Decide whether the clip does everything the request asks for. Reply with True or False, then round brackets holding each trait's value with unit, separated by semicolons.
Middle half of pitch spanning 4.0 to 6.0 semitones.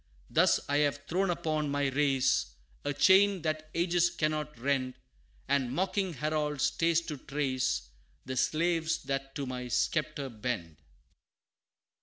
False (3.4 semitones)